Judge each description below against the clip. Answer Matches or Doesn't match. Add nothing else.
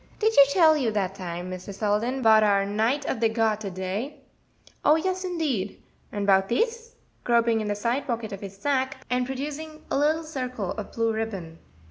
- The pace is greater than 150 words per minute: Matches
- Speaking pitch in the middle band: Doesn't match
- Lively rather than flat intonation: Matches